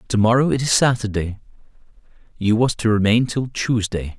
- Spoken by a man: Yes, male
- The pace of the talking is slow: Yes, slow, 130 wpm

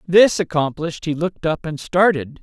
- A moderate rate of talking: Yes, average, 175 wpm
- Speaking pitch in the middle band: Yes, medium, 165 Hz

